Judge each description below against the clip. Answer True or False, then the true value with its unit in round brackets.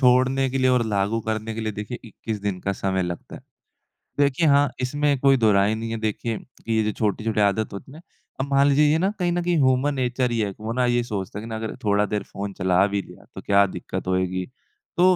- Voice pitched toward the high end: False (115 Hz)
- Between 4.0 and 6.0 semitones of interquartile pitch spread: True (4.6 semitones)